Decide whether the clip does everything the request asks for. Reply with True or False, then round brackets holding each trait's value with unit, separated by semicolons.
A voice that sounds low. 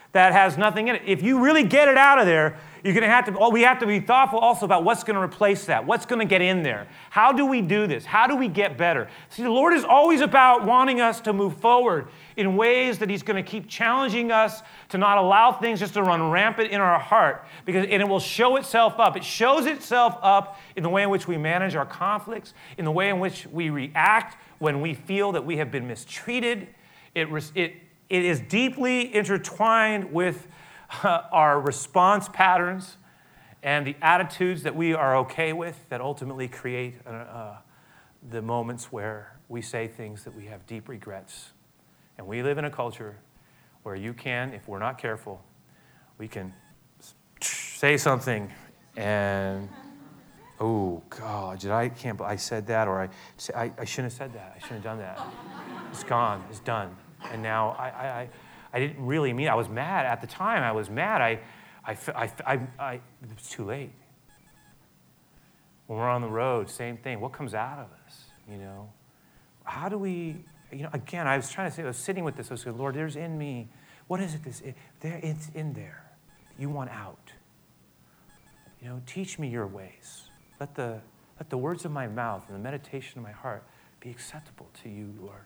False (155 Hz)